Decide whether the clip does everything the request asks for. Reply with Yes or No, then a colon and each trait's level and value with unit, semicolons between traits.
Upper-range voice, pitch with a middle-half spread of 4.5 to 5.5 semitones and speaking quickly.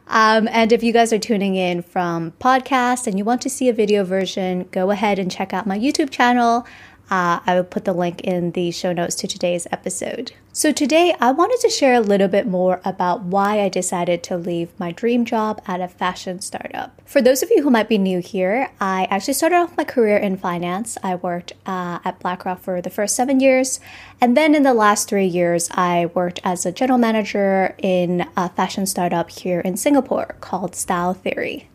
Yes: high, 195 Hz; average, 4.8 semitones; fast, 210 wpm